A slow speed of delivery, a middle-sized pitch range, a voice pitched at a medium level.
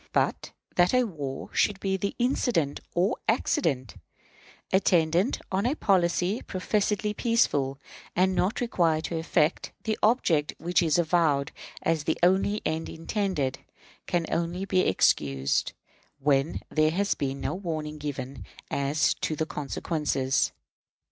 Yes: slow, 130 wpm; average, 4.7 semitones; medium, 170 Hz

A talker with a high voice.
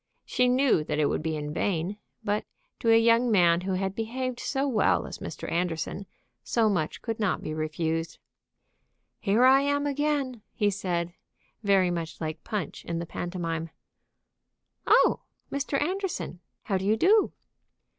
Yes: high, 200 Hz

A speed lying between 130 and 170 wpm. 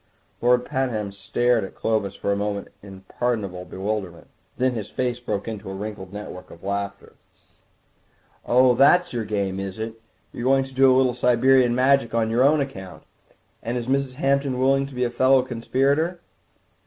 No: average, 180 wpm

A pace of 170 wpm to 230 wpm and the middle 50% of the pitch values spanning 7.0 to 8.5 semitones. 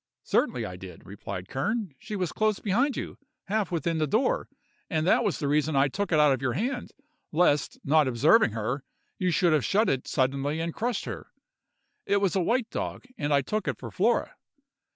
Yes: average, 195 wpm; wide, 7.5 semitones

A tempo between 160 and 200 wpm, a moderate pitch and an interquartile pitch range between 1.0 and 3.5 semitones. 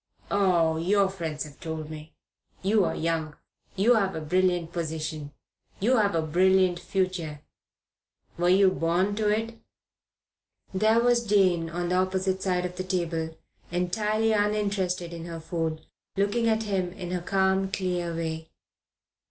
No: average, 145 wpm; medium, 180 Hz; average, 3.2 semitones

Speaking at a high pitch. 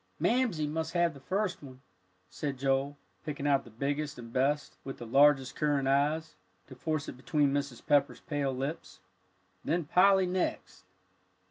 No: medium, 145 Hz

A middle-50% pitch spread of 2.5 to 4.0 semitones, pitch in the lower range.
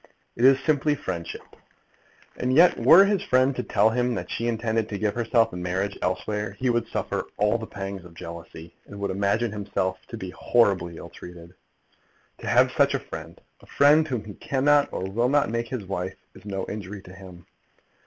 No: average, 4.8 semitones; low, 105 Hz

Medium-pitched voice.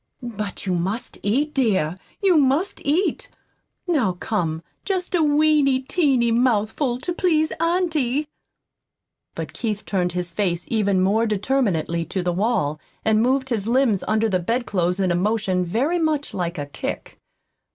No: high, 225 Hz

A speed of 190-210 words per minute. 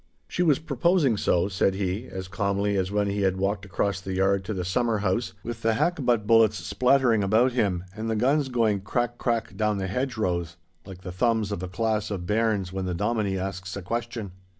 Yes: fast, 205 wpm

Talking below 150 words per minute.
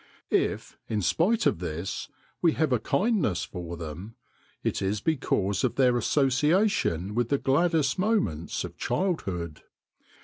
Yes: slow, 135 wpm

